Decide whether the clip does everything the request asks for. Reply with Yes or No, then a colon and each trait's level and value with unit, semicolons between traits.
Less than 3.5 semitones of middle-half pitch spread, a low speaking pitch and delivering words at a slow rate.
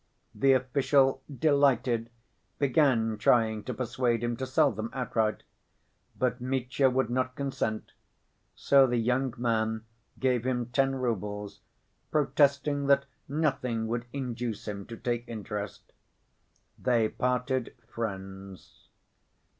Yes: average, 2.9 semitones; low, 125 Hz; slow, 115 wpm